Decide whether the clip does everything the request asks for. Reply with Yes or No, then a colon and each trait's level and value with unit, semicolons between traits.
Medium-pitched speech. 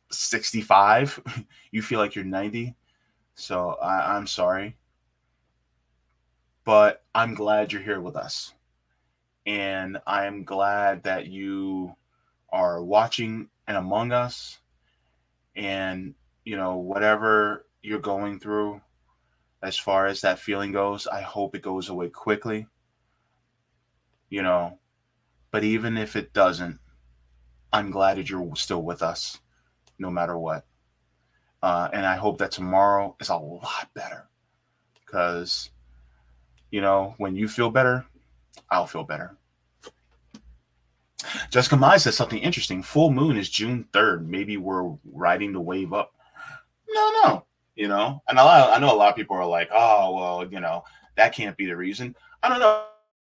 No: very low, 95 Hz